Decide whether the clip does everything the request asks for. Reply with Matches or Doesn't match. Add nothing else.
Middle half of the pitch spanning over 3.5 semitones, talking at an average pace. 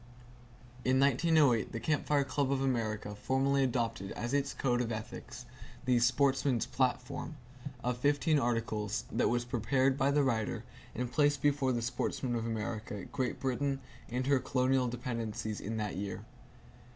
Doesn't match